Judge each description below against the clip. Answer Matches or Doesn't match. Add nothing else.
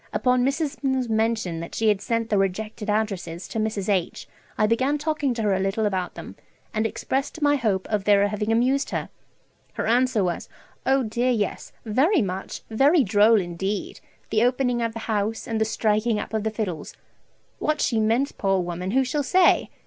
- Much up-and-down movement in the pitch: Doesn't match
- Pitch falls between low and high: Doesn't match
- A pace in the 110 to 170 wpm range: Doesn't match